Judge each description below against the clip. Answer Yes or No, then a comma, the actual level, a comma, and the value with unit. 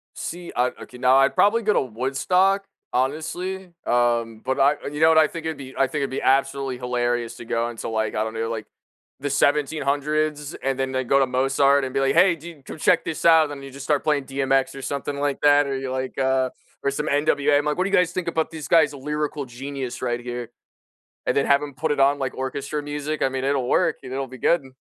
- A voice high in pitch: No, medium, 140 Hz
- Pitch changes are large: No, narrow, 2.6 semitones